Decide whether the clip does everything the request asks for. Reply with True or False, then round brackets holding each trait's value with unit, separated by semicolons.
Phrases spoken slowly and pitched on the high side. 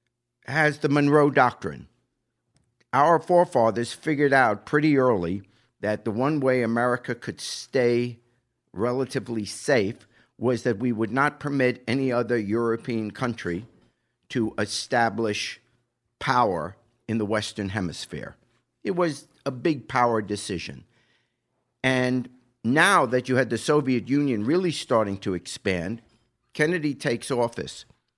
False (120 wpm; 120 Hz)